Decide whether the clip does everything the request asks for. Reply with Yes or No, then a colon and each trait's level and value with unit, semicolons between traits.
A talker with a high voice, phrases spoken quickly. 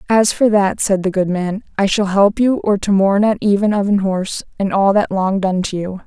Yes: high, 200 Hz; fast, 245 wpm